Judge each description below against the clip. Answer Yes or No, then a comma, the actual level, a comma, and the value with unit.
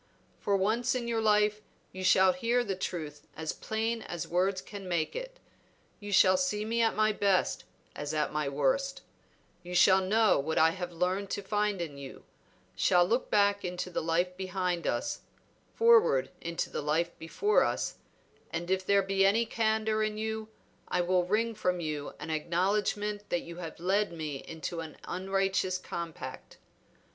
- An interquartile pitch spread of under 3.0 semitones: No, average, 3.8 semitones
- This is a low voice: No, high, 190 Hz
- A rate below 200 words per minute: Yes, average, 170 wpm